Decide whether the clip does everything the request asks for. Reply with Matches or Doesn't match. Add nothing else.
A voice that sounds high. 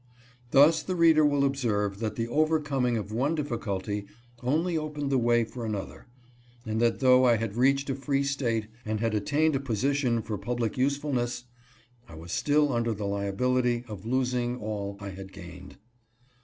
Doesn't match